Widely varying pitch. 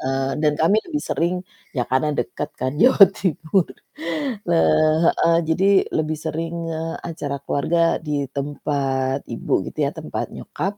No: average, 3.4 semitones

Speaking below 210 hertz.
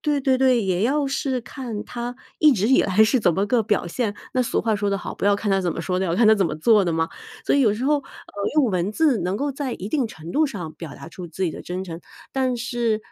No: high, 215 Hz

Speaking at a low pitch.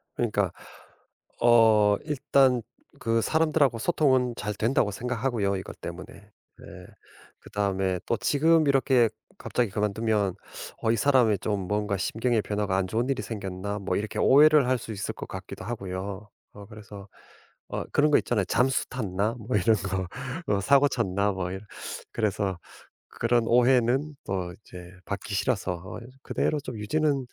Yes: low, 110 Hz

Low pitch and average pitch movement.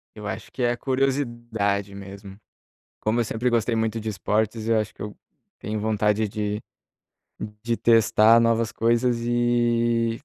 No: low, 115 Hz; narrow, 1.9 semitones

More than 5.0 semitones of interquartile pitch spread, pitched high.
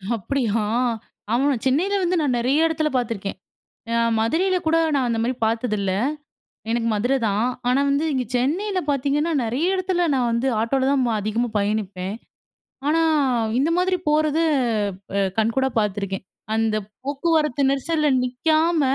Yes: wide, 5.4 semitones; very high, 265 Hz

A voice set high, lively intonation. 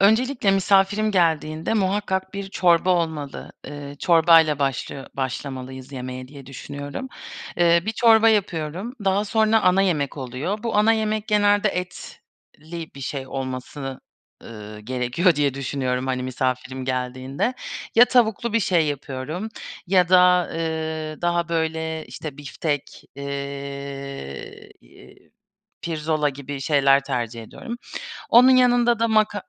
No: medium, 160 Hz; wide, 6.3 semitones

